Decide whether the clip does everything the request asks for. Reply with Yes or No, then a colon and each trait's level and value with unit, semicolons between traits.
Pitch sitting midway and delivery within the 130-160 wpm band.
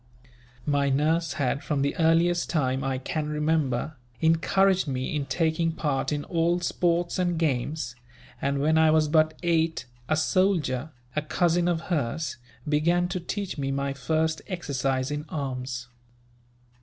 Yes: medium, 155 Hz; average, 145 wpm